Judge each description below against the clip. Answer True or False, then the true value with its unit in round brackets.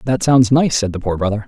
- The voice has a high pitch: False (115 Hz)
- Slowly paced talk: False (285 wpm)